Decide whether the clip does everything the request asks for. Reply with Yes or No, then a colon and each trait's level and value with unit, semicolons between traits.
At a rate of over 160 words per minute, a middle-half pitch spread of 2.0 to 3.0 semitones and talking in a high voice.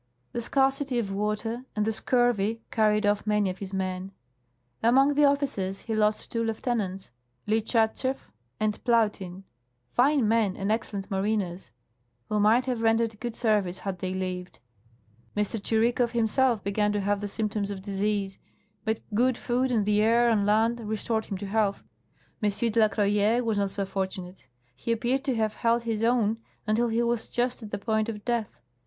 Yes: average, 180 wpm; average, 2.7 semitones; high, 215 Hz